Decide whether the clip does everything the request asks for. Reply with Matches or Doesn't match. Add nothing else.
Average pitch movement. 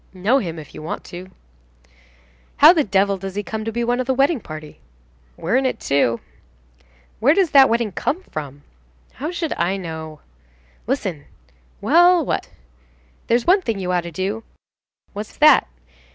Doesn't match